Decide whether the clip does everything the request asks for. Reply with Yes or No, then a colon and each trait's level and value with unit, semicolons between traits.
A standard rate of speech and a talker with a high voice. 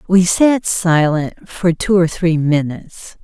No: average, 150 wpm; medium, 175 Hz